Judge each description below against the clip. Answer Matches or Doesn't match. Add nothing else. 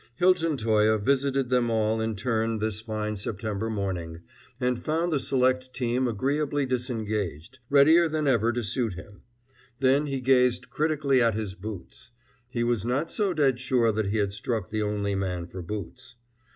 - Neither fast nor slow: Matches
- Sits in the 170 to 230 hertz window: Doesn't match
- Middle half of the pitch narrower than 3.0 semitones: Doesn't match